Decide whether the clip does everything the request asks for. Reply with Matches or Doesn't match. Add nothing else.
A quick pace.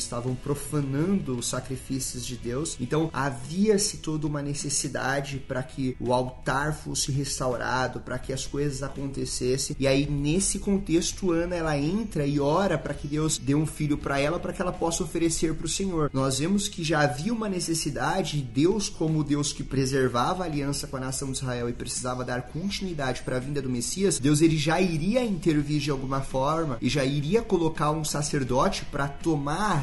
Matches